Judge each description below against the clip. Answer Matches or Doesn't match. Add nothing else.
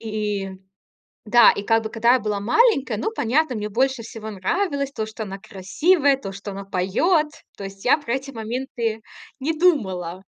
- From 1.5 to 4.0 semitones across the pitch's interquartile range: Doesn't match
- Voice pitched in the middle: Doesn't match